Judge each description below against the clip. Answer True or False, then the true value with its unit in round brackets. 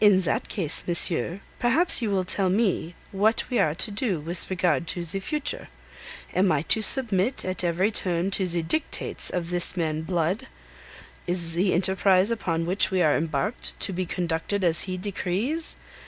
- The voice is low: False (185 Hz)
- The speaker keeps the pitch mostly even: False (3.1 semitones)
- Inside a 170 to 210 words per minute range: True (175 wpm)